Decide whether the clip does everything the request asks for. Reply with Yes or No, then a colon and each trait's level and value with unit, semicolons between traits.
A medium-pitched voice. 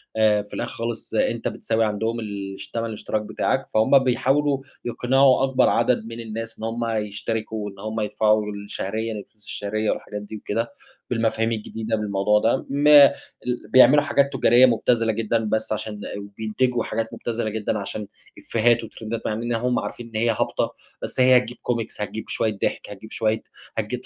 No: low, 110 Hz